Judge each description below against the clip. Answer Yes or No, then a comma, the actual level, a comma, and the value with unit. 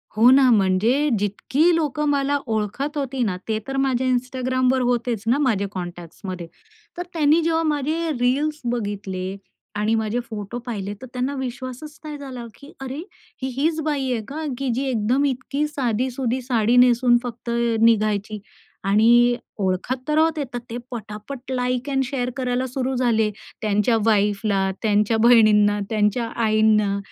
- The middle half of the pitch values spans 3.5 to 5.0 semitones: Yes, average, 4.0 semitones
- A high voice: Yes, high, 245 Hz